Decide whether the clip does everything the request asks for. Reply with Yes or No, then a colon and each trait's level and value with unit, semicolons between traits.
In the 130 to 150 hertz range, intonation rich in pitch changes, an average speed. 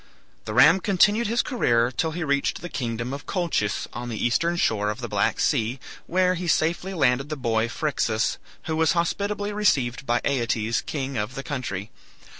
Yes: medium, 140 Hz; wide, 6.7 semitones; average, 180 wpm